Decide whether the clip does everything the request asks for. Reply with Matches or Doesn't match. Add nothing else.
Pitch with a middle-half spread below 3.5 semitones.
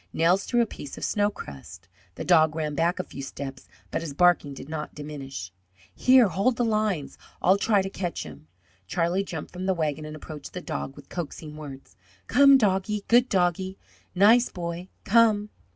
Doesn't match